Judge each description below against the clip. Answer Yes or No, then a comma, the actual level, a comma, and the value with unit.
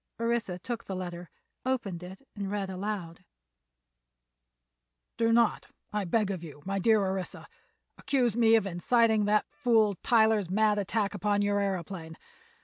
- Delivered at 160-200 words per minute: No, average, 140 wpm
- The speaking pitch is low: No, high, 205 Hz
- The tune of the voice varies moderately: Yes, average, 3.1 semitones